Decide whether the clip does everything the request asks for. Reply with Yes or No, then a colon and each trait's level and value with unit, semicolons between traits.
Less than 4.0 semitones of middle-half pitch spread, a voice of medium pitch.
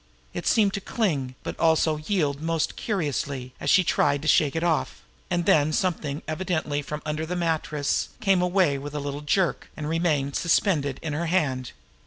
Yes: average, 3.3 semitones; medium, 155 Hz